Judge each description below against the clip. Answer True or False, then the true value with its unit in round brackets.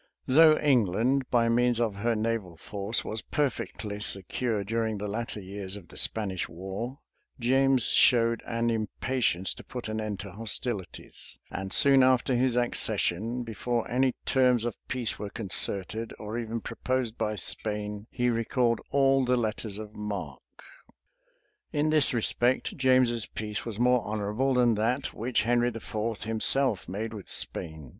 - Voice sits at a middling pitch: False (115 Hz)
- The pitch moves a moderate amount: True (3.0 semitones)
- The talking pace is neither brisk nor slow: True (150 wpm)